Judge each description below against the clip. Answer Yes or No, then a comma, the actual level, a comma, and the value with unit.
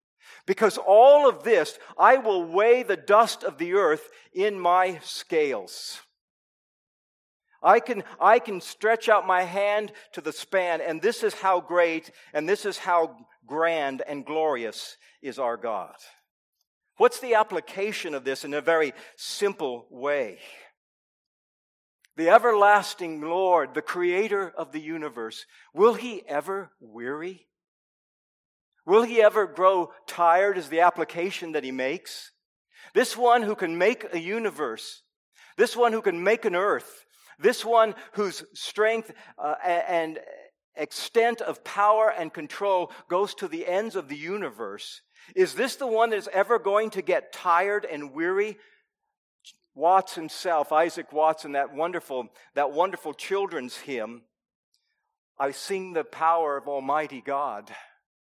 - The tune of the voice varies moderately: No, wide, 6.0 semitones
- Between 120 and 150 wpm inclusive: Yes, average, 140 wpm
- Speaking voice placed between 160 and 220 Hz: Yes, high, 190 Hz